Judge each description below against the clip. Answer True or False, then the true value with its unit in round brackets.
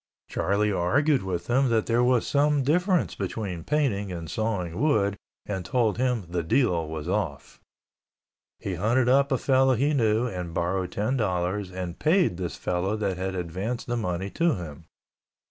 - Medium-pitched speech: False (105 Hz)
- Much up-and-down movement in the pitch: True (6.0 semitones)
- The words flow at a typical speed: True (165 wpm)